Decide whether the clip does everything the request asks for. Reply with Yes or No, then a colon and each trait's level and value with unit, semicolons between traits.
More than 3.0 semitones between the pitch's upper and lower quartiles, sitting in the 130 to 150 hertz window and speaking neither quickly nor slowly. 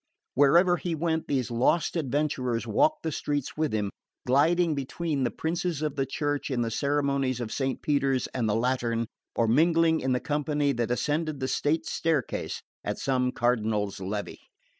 Yes: average, 4.1 semitones; medium, 140 Hz; average, 165 wpm